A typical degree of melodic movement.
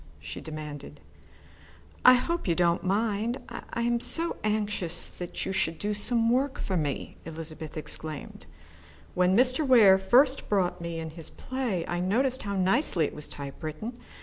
No: wide, 6.4 semitones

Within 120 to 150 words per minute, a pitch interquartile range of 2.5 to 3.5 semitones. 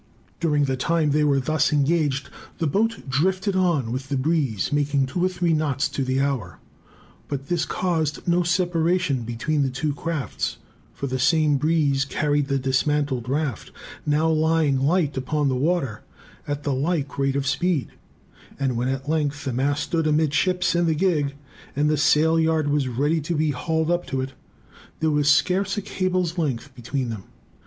No: average, 175 wpm; average, 3.2 semitones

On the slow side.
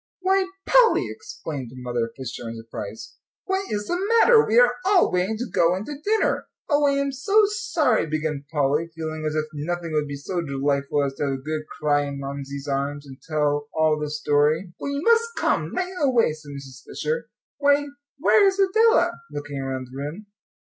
No: average, 190 wpm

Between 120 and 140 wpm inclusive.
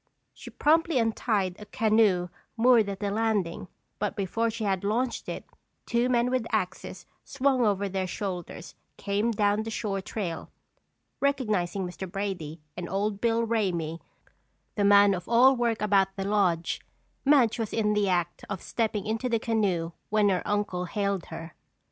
No: average, 160 wpm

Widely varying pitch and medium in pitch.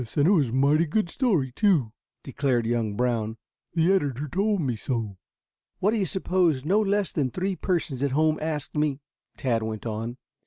Yes: wide, 6.9 semitones; medium, 145 Hz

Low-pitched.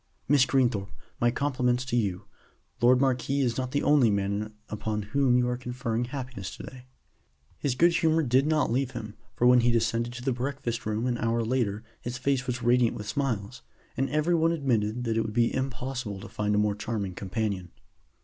Yes: low, 120 Hz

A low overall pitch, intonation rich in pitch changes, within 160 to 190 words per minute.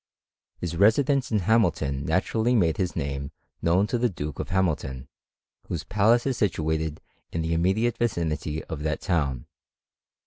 No: very low, 85 Hz; wide, 6.1 semitones; average, 145 wpm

